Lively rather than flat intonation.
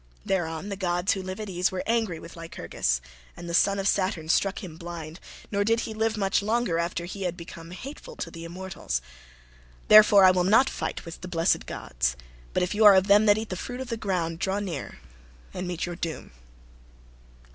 No: average, 3.3 semitones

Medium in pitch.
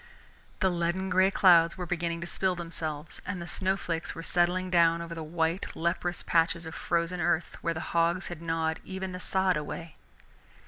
Yes: medium, 170 Hz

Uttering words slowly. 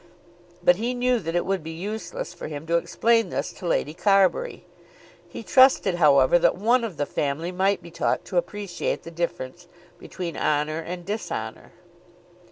No: average, 170 wpm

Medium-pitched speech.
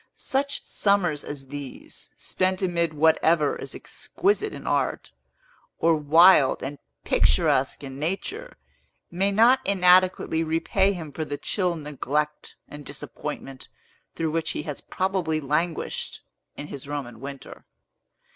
Yes: medium, 160 Hz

